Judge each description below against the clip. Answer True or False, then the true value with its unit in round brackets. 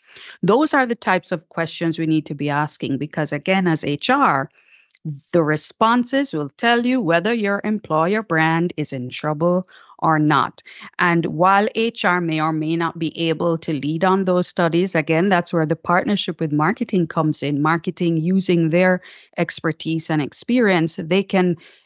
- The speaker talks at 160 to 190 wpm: True (165 wpm)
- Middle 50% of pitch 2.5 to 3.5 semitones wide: True (3.0 semitones)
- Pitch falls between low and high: True (170 Hz)